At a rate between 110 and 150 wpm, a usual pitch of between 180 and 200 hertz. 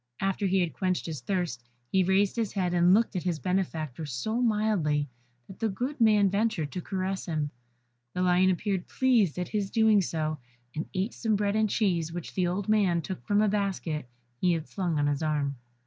No: average, 200 wpm; medium, 185 Hz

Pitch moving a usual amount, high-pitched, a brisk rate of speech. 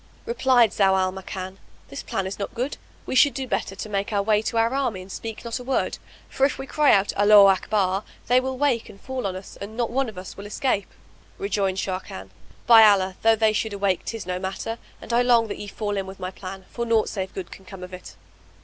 Yes: average, 3.6 semitones; high, 205 Hz; fast, 240 wpm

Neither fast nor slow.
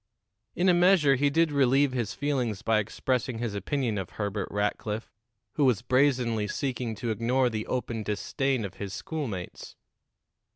Yes: average, 155 wpm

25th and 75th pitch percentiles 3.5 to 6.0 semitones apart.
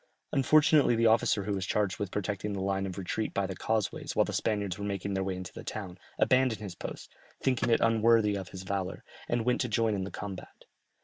No: average, 2.8 semitones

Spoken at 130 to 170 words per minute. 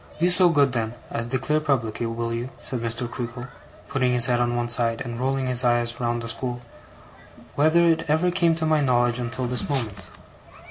No: average, 195 wpm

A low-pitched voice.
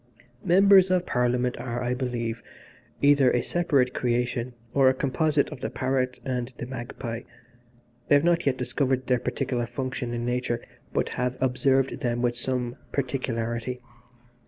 Yes: low, 125 Hz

